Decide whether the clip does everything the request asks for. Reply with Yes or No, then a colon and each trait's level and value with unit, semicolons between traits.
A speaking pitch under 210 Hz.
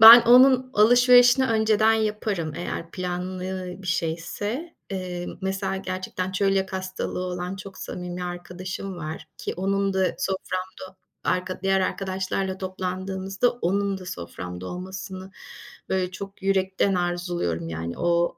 Yes: high, 190 Hz